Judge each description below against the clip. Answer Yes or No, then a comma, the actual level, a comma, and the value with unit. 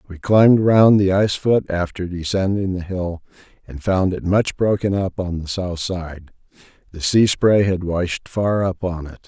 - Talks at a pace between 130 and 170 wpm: No, average, 190 wpm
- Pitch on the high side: No, very low, 95 Hz